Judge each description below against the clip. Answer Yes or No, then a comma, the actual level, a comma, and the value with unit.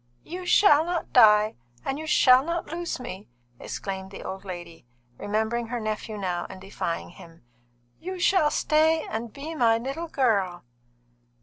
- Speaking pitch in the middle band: No, high, 235 Hz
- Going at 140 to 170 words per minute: Yes, average, 150 wpm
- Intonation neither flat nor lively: No, wide, 8.2 semitones